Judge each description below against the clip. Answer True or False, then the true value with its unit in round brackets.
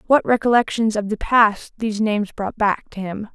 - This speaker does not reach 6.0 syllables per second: True (5.2 syllables/s)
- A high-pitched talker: True (215 Hz)